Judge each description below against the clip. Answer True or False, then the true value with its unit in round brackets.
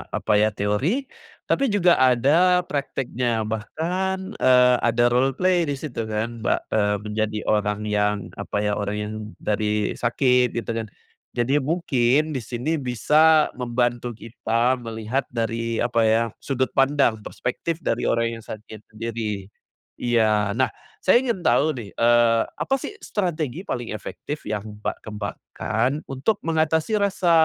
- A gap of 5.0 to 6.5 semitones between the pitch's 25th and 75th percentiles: True (5.3 semitones)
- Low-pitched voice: True (120 Hz)